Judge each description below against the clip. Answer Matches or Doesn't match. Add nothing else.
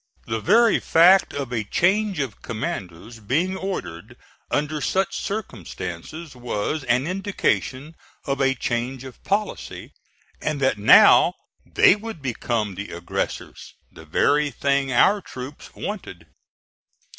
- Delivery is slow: Matches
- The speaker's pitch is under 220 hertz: Matches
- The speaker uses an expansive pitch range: Matches